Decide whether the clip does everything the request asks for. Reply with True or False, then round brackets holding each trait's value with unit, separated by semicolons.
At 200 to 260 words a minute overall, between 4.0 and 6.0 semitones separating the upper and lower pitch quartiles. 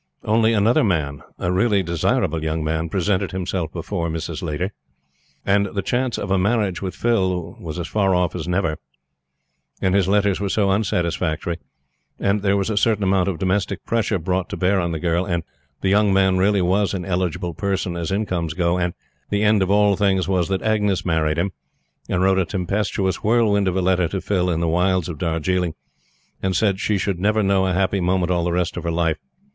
False (205 wpm; 2.5 semitones)